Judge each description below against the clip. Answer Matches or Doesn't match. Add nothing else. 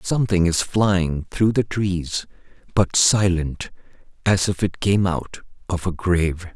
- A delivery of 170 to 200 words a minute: Doesn't match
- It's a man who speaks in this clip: Matches